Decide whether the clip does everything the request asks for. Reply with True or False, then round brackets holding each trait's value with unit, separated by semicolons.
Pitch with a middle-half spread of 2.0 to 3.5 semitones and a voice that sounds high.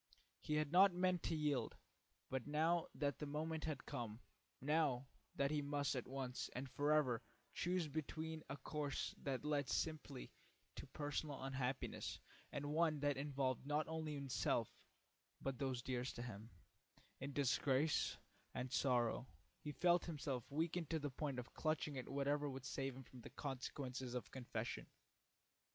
False (2.9 semitones; 140 Hz)